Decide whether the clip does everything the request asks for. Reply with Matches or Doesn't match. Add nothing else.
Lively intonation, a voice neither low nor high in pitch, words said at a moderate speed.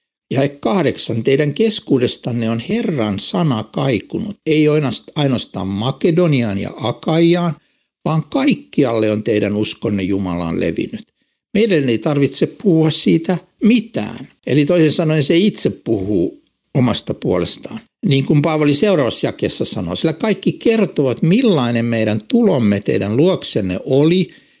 Matches